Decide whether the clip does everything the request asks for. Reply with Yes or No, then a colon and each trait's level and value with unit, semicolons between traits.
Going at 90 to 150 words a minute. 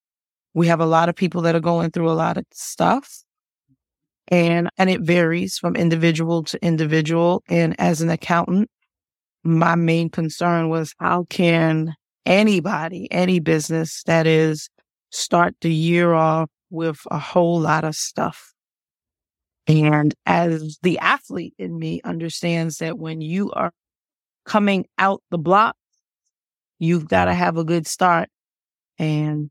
Yes: average, 140 wpm